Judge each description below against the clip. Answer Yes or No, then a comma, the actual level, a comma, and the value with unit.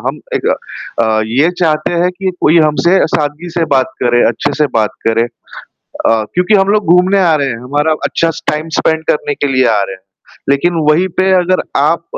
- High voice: No, medium, 155 Hz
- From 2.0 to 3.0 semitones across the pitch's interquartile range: No, average, 4.8 semitones